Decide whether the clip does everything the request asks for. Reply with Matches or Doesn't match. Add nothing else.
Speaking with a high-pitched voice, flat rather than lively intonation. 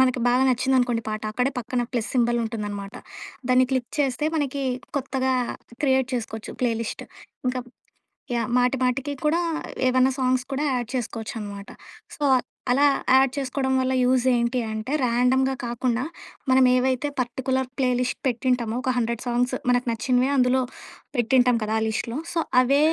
Matches